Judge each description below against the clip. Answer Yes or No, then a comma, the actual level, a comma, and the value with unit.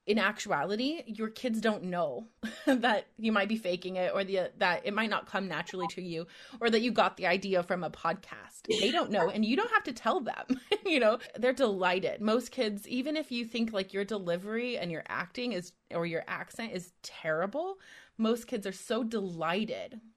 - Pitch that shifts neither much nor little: Yes, average, 4.7 semitones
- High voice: Yes, high, 220 Hz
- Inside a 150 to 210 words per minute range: Yes, average, 200 wpm